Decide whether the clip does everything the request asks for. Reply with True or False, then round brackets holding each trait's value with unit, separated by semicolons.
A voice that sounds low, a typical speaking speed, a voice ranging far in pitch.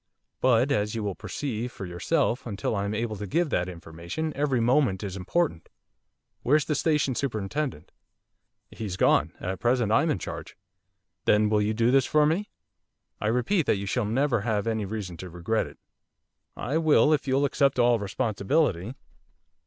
True (115 Hz; 170 wpm; 5.7 semitones)